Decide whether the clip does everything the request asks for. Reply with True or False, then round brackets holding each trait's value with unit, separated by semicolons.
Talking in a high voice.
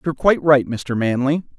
False (140 Hz)